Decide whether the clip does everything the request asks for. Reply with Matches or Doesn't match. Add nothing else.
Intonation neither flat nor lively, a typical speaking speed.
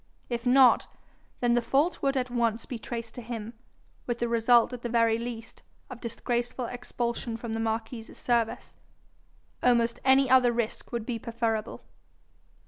Doesn't match